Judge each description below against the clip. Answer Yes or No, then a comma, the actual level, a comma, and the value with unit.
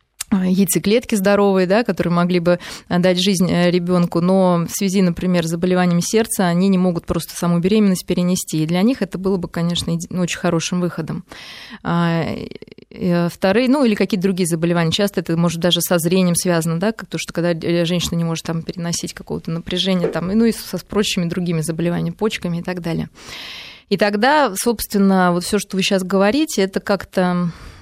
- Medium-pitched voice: Yes, medium, 180 Hz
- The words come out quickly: Yes, fast, 175 wpm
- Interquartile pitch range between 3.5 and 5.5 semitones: No, narrow, 2.6 semitones